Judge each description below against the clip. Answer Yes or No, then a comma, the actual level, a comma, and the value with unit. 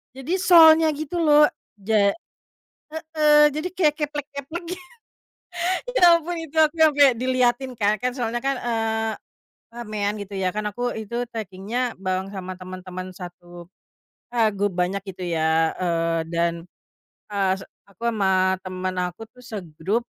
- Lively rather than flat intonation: Yes, wide, 7.3 semitones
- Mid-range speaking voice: No, high, 220 Hz